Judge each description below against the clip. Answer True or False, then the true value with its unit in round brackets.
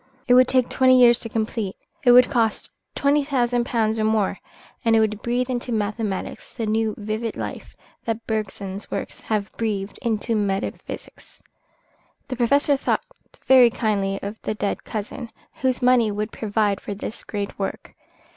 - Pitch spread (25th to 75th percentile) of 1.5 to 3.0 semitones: True (2.7 semitones)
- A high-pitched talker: True (225 Hz)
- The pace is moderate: True (160 wpm)